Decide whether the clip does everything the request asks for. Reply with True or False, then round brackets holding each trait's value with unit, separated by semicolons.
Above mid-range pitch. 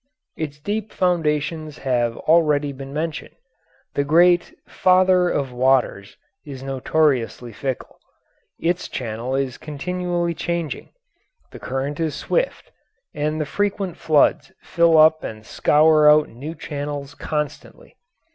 False (150 Hz)